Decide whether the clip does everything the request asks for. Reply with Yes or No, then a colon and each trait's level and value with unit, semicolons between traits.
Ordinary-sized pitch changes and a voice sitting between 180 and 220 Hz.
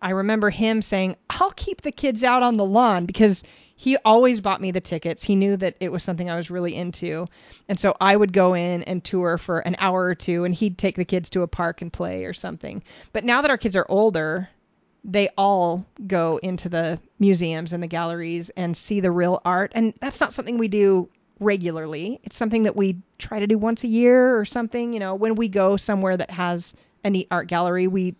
Yes: average, 3.6 semitones; high, 190 Hz